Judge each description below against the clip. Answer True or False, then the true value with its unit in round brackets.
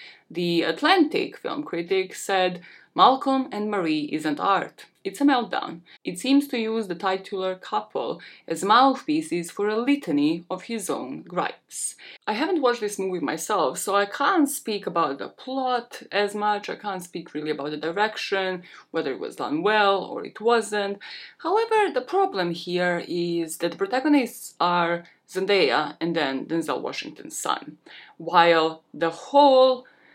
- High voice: True (205 Hz)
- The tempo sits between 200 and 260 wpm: False (155 wpm)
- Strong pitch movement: True (7.5 semitones)